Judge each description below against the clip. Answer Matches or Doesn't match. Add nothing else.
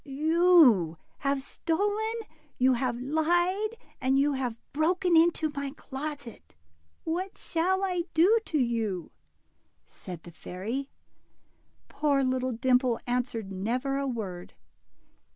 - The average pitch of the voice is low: Doesn't match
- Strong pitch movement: Matches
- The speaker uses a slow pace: Matches